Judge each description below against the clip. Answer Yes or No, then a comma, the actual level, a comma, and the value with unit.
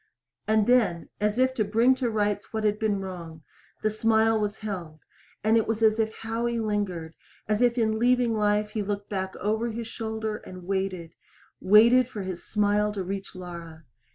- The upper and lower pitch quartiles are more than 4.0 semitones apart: No, narrow, 2.5 semitones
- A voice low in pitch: No, high, 210 Hz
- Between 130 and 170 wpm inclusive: No, average, 180 wpm